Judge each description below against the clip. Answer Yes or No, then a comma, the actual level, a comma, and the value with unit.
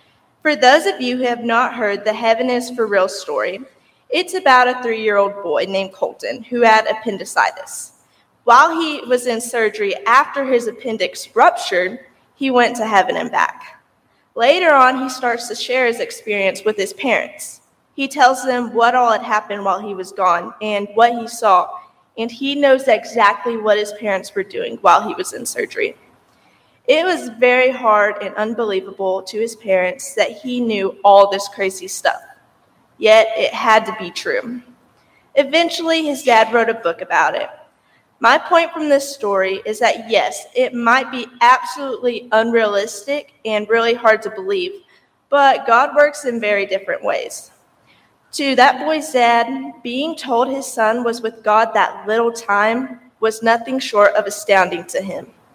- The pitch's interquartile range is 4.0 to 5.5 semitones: Yes, average, 4.5 semitones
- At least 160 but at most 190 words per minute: Yes, average, 170 wpm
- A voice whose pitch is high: Yes, high, 235 Hz